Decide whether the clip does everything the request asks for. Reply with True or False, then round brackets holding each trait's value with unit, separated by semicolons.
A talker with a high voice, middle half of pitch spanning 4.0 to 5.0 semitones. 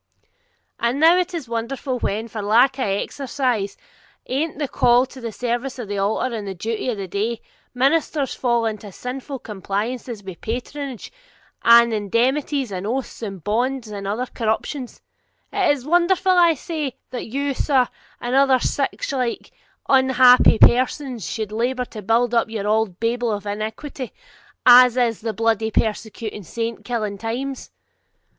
False (240 Hz; 3.4 semitones)